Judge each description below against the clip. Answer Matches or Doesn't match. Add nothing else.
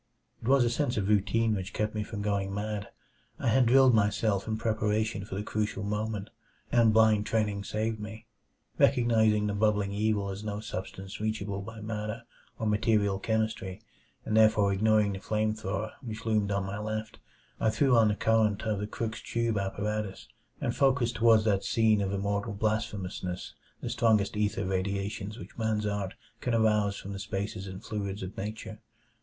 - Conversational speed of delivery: Matches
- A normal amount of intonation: Doesn't match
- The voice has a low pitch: Matches